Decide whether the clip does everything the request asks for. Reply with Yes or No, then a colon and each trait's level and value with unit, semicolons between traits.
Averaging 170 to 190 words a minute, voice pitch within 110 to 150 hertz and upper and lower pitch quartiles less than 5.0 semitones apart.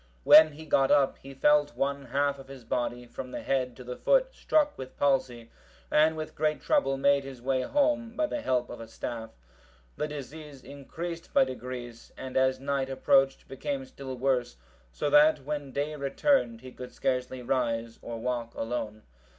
Yes: average, 180 wpm; low, 135 Hz; average, 2.9 semitones